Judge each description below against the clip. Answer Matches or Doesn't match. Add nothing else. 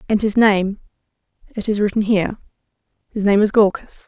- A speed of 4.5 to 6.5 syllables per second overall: Matches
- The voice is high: Matches